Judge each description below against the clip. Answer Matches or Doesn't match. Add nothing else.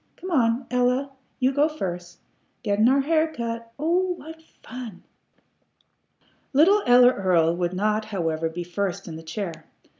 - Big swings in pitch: Matches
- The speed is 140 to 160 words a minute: Matches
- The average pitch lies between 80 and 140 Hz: Doesn't match